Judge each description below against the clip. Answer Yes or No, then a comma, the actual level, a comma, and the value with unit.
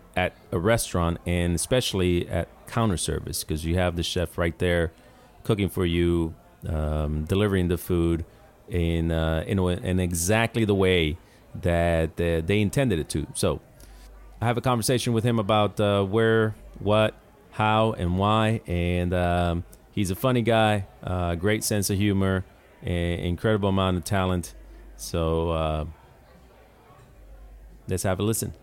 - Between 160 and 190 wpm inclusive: No, average, 150 wpm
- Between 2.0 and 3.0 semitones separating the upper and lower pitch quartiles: No, average, 3.9 semitones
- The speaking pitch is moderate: No, very low, 90 Hz